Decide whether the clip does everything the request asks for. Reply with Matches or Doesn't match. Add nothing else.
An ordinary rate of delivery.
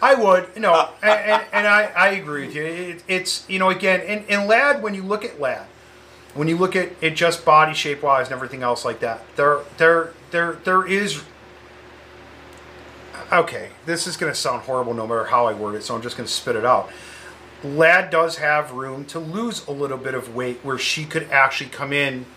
Doesn't match